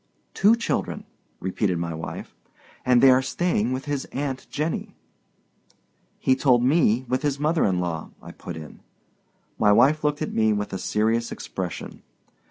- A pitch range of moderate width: No, wide, 5.9 semitones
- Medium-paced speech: Yes, average, 160 wpm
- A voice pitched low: Yes, low, 125 Hz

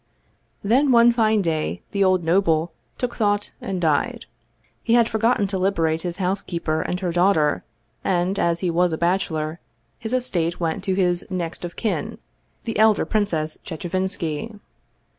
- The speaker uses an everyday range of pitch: Yes, average, 3.7 semitones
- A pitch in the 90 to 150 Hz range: No, medium, 185 Hz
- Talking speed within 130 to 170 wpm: Yes, average, 155 wpm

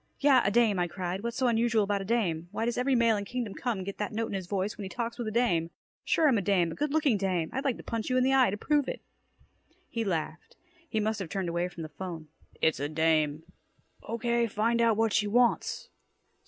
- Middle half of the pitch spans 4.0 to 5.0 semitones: Yes, average, 4.7 semitones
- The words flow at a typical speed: No, fast, 250 wpm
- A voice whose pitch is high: Yes, high, 210 Hz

